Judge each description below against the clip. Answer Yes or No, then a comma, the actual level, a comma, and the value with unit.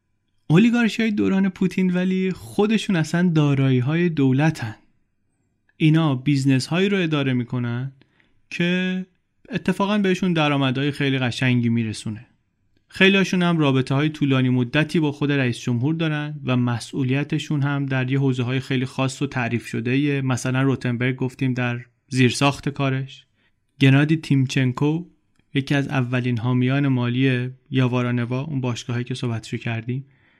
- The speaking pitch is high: No, low, 135 Hz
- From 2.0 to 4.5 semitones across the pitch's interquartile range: Yes, average, 3.6 semitones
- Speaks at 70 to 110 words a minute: No, average, 130 wpm